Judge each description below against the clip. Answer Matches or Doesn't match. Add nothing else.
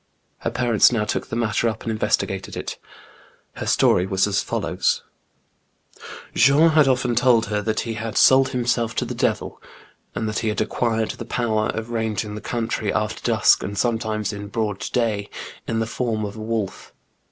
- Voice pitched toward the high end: Doesn't match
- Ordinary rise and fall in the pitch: Doesn't match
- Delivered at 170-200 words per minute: Matches